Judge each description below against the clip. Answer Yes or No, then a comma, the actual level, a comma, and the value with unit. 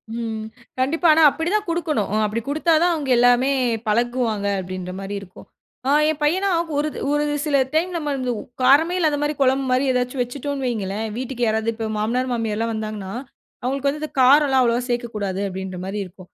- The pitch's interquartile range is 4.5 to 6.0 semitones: Yes, average, 5.0 semitones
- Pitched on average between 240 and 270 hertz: Yes, very high, 250 Hz